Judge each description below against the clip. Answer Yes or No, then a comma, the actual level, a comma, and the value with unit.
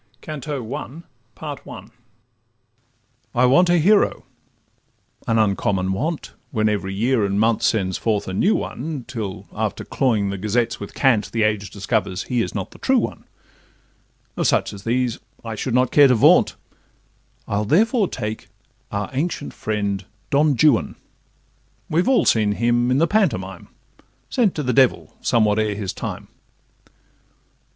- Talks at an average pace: Yes, average, 150 wpm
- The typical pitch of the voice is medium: No, low, 115 Hz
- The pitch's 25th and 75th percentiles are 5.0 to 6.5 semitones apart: Yes, wide, 5.6 semitones